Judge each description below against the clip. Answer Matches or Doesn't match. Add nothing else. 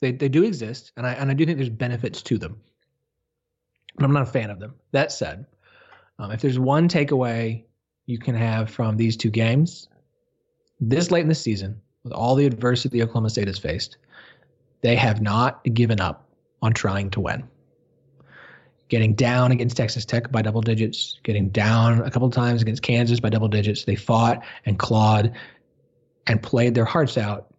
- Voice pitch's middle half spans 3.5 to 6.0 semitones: Doesn't match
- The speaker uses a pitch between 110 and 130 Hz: Matches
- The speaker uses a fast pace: Doesn't match